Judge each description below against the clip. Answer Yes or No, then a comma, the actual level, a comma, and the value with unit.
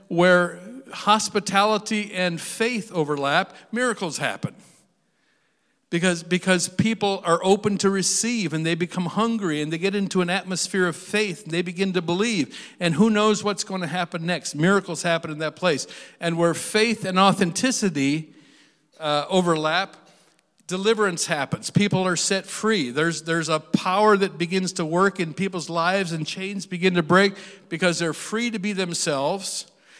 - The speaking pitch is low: No, medium, 185 Hz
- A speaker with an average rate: Yes, average, 160 wpm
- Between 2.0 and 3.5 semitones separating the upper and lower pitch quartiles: Yes, average, 3.0 semitones